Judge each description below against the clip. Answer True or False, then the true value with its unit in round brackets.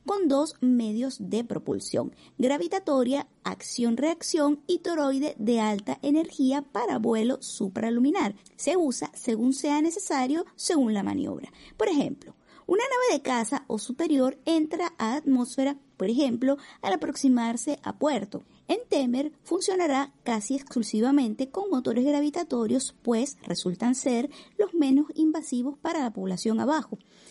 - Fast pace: False (125 wpm)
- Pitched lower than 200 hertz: False (275 Hz)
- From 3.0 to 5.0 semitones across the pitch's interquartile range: True (4.3 semitones)